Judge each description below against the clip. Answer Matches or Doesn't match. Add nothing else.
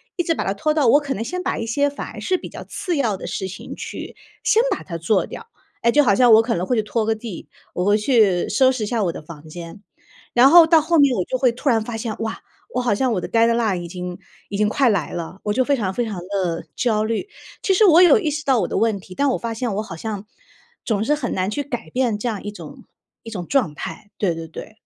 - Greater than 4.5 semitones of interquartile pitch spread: Matches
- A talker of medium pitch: Doesn't match